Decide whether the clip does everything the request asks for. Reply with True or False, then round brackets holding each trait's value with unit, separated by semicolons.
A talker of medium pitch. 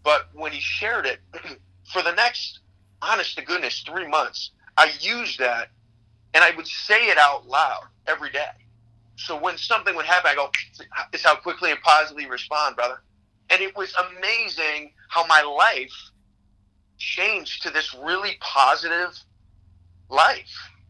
False (120 Hz)